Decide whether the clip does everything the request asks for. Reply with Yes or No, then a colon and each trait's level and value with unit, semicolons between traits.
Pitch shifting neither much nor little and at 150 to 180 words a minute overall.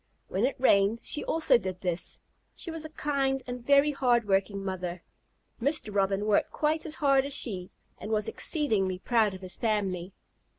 No: wide, 6.4 semitones; average, 175 wpm